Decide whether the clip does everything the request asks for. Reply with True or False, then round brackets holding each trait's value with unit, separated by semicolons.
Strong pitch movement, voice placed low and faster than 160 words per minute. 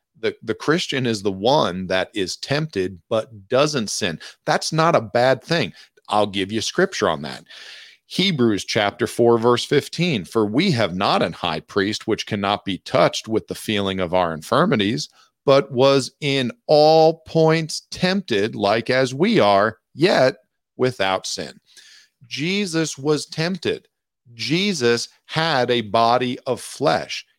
False (6.5 semitones; 125 Hz; 145 wpm)